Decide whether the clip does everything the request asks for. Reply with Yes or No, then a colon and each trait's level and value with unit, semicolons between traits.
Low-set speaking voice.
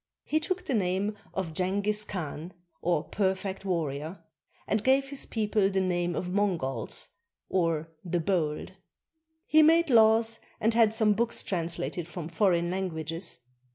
No: high, 190 Hz